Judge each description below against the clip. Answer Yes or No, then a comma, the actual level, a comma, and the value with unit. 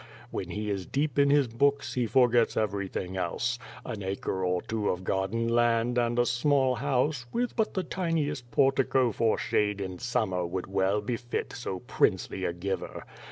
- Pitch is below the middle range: Yes, low, 120 Hz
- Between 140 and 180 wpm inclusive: Yes, average, 170 wpm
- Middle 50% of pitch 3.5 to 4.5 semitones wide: No, average, 5.1 semitones